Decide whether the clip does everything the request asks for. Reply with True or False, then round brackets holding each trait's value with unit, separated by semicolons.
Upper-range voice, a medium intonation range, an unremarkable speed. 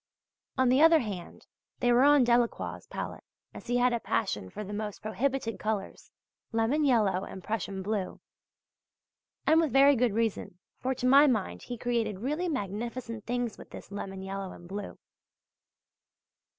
True (230 Hz; 3.9 semitones; 160 wpm)